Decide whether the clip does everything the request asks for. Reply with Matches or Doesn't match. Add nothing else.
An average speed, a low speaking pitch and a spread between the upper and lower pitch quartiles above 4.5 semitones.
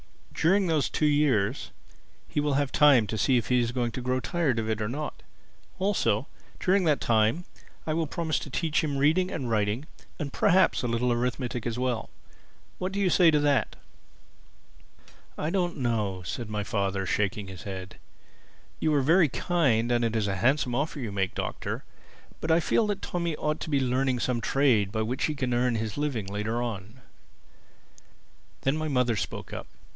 Matches